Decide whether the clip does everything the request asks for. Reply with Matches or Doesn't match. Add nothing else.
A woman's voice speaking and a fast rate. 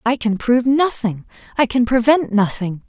Doesn't match